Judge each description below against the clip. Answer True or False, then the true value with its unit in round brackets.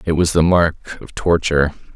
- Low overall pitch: True (80 Hz)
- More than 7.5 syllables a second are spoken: False (5.6 syllables/s)